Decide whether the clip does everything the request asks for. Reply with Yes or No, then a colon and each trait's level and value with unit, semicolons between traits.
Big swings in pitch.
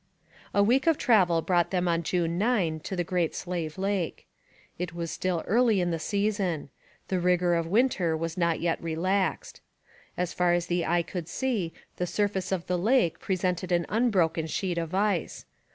No: average, 2.7 semitones